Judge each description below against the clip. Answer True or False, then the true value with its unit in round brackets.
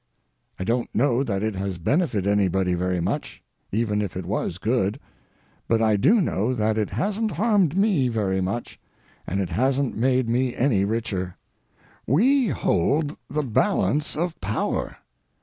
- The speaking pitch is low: True (115 Hz)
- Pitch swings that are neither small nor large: False (6.6 semitones)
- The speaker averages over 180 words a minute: False (150 wpm)